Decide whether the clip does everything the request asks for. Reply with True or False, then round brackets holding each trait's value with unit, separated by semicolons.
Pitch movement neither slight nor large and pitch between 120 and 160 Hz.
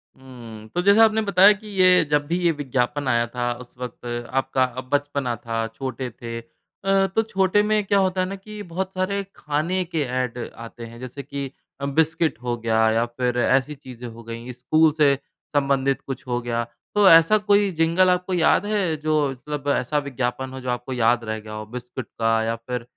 False (6.7 semitones; 135 Hz)